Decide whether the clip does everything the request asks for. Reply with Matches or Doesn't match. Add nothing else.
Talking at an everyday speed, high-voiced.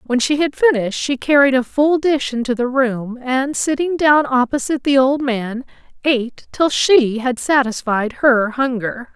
Matches